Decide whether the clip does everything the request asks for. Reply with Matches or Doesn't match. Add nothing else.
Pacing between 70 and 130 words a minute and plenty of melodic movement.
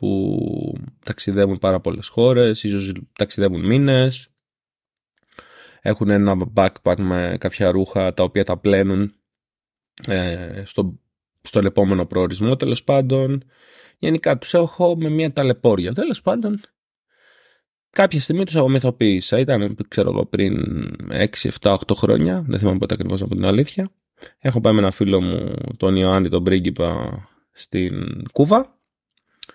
Matches